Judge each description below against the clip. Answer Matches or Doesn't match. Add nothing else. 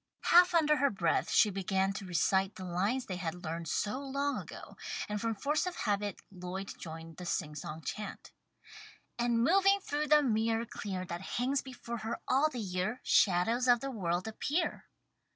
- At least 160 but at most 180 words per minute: Matches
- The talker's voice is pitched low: Doesn't match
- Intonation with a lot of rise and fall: Matches